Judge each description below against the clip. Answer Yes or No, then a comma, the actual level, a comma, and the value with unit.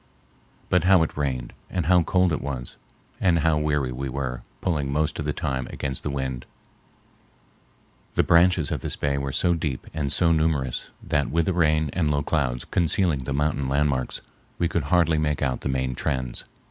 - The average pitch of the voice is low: Yes, very low, 75 Hz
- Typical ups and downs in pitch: Yes, average, 3.6 semitones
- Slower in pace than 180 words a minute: No, average, 185 wpm